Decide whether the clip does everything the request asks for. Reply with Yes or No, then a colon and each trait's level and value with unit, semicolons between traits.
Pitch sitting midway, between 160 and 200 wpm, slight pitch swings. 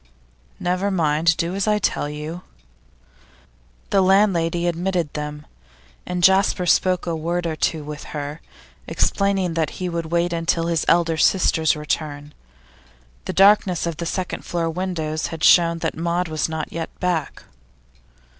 No: medium, 170 Hz; average, 145 wpm; narrow, 2.3 semitones